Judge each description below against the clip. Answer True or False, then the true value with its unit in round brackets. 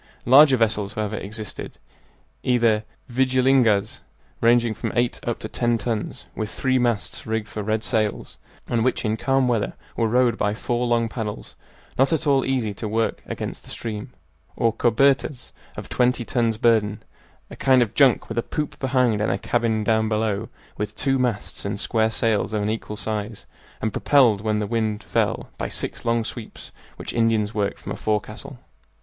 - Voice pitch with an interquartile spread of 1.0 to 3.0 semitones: True (2.4 semitones)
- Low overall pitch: True (115 Hz)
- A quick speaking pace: False (175 wpm)